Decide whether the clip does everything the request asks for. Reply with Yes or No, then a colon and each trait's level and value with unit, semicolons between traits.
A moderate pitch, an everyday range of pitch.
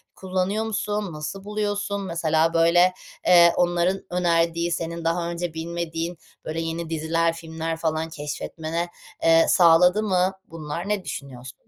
No: medium, 170 Hz; narrow, 1.8 semitones